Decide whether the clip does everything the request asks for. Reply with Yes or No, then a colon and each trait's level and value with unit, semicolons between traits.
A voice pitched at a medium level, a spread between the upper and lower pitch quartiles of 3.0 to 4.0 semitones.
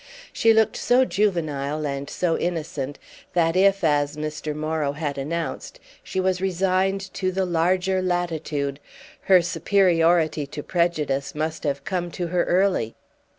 Yes: medium, 170 Hz; average, 3.7 semitones